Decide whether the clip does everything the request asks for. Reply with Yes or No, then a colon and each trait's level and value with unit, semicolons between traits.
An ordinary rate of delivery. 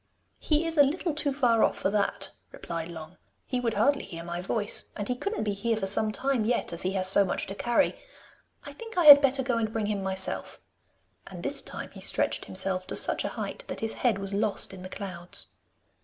No: fast, 230 wpm